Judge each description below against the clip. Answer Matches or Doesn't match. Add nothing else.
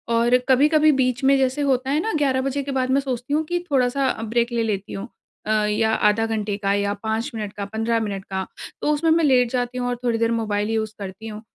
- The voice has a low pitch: Doesn't match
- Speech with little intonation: Doesn't match